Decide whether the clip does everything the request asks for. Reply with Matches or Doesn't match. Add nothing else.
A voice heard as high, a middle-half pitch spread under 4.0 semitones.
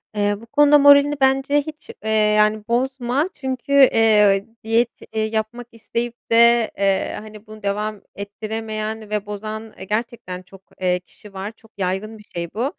Matches